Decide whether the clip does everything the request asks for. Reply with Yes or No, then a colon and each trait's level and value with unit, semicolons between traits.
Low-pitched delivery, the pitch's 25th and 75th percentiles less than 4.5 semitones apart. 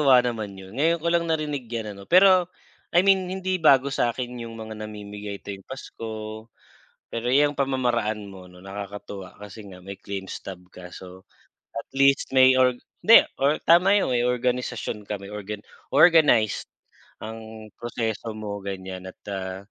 No: low, 115 Hz; average, 5.2 semitones